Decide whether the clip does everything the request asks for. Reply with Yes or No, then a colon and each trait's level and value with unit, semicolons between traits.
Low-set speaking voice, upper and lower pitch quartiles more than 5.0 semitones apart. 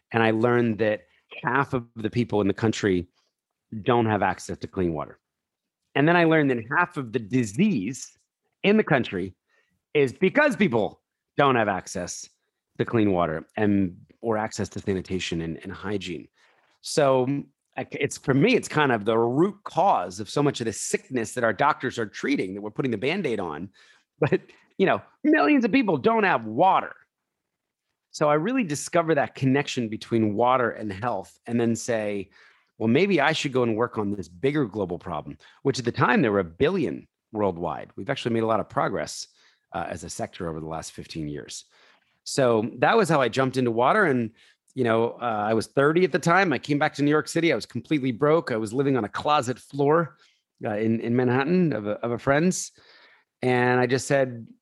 Yes: low, 125 Hz; wide, 5.5 semitones